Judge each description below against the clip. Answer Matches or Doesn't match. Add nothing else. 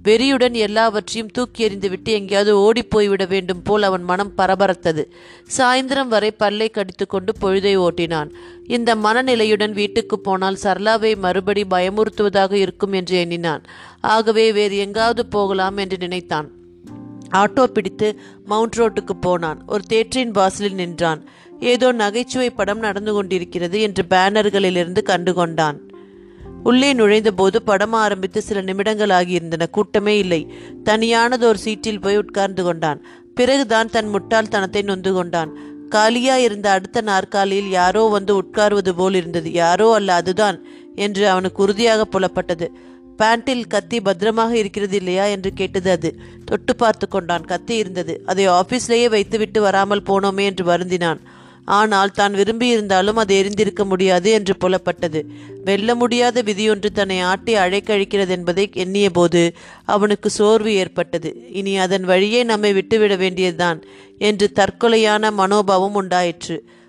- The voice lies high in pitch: Matches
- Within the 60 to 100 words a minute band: Doesn't match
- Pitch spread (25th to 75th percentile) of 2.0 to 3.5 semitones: Matches